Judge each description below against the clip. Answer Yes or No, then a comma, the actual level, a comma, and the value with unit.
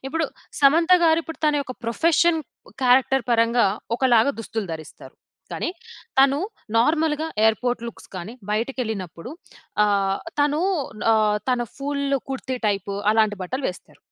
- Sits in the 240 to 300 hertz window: Yes, very high, 250 Hz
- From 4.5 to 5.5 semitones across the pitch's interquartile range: Yes, average, 5.0 semitones